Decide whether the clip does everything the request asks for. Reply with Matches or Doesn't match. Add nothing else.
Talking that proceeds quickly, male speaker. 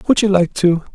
Matches